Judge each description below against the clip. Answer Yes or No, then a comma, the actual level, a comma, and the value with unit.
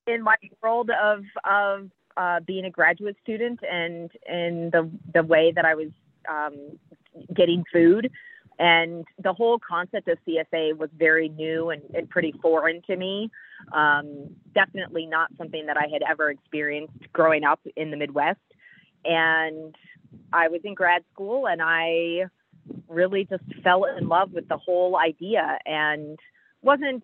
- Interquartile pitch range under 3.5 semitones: Yes, average, 2.9 semitones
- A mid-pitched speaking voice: Yes, medium, 170 Hz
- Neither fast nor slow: Yes, average, 155 wpm